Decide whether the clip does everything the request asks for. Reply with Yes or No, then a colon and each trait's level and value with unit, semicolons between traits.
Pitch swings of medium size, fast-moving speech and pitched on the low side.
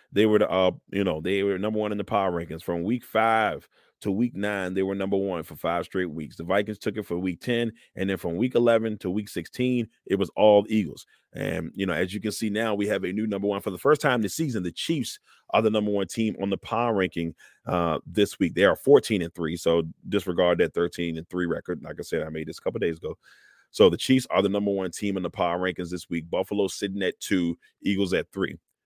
Yes: average, 3.3 semitones; fast, 260 wpm; low, 100 Hz